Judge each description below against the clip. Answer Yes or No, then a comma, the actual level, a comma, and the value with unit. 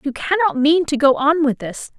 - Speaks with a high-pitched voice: Yes, very high, 295 Hz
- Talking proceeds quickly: Yes, fast, 240 wpm